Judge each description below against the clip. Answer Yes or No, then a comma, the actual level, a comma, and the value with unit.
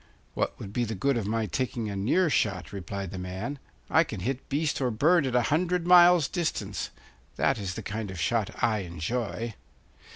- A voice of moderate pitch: No, low, 115 Hz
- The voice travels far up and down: Yes, wide, 6.2 semitones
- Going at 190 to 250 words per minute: Yes, average, 195 wpm